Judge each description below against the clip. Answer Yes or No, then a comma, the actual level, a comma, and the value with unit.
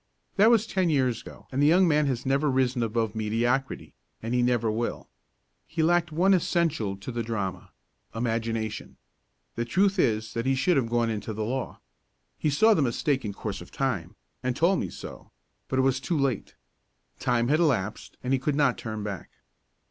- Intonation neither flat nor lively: Yes, average, 5.0 semitones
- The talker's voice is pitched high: No, low, 130 Hz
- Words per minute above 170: Yes, average, 190 wpm